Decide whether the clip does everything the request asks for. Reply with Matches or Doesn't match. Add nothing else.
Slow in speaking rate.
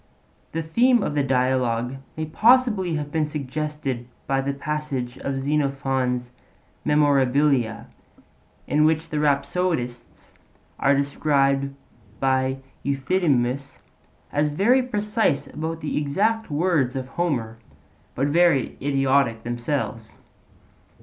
Matches